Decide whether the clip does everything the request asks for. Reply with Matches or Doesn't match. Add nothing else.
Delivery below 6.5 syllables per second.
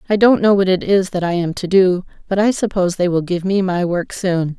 Matches